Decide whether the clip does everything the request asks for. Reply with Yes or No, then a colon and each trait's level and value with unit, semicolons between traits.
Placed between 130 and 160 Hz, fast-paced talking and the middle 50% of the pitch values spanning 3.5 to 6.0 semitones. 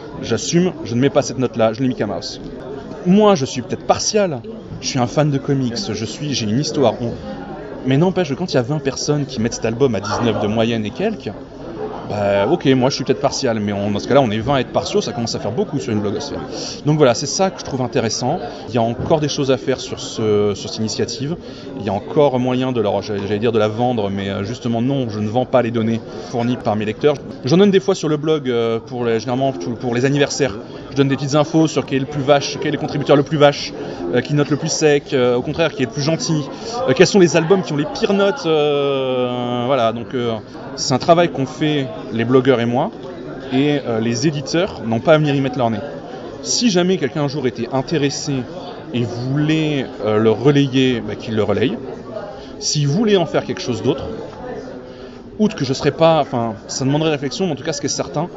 Yes: low, 135 Hz; fast, 245 wpm; average, 4.0 semitones